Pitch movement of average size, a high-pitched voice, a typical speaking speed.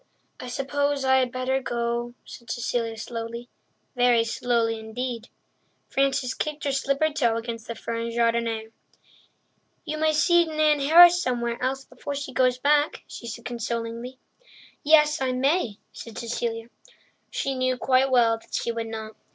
Yes: average, 3.0 semitones; very high, 250 Hz; average, 145 wpm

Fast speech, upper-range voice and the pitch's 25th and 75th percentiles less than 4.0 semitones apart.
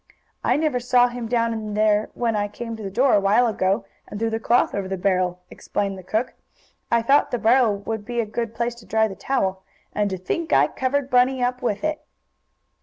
Yes: fast, 225 wpm; high, 225 Hz; average, 3.3 semitones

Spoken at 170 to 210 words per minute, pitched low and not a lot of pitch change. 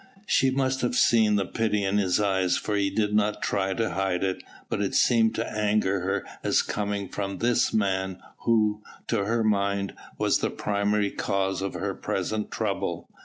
Yes: average, 180 wpm; low, 105 Hz; narrow, 1.9 semitones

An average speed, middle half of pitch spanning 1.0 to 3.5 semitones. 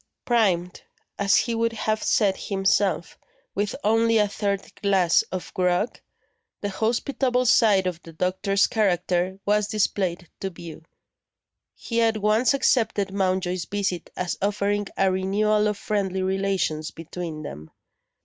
No: slow, 130 wpm; narrow, 2.6 semitones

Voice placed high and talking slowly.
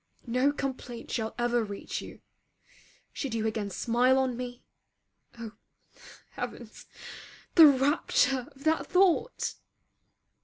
Yes: very high, 250 Hz; slow, 110 wpm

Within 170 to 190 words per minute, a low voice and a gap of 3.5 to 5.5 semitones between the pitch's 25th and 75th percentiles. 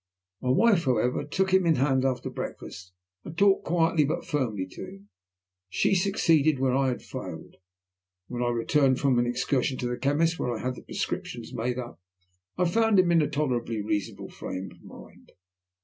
Yes: average, 185 wpm; low, 130 Hz; average, 5.2 semitones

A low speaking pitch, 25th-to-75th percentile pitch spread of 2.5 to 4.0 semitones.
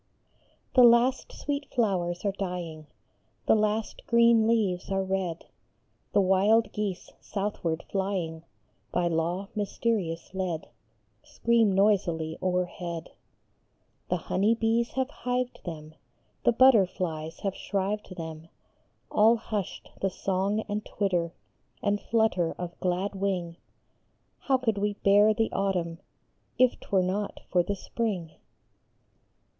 No: high, 195 Hz; average, 3.7 semitones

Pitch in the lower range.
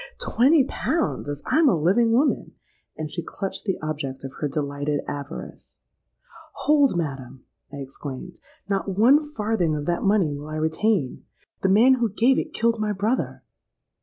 No: medium, 185 Hz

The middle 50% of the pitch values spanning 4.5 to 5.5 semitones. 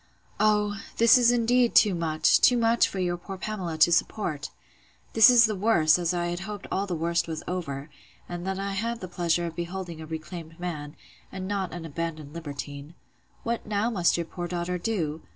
No: average, 4.1 semitones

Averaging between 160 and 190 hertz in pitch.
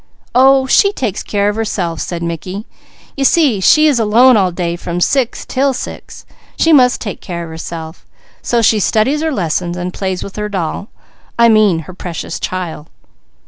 No: high, 205 Hz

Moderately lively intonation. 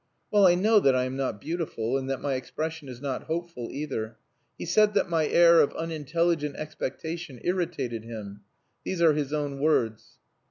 Yes: average, 4.6 semitones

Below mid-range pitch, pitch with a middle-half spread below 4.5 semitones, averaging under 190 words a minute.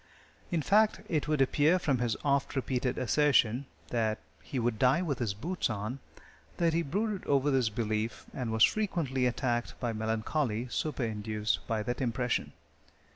No: low, 125 Hz; average, 4.8 semitones; average, 155 wpm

